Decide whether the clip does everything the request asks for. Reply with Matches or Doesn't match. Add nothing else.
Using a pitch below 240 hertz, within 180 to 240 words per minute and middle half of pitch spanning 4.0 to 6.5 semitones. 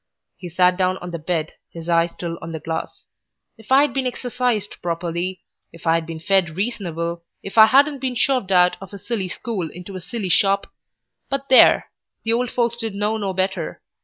Matches